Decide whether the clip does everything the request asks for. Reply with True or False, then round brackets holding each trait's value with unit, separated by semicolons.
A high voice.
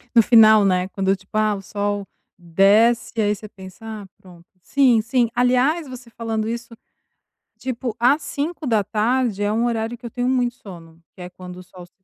True (220 Hz)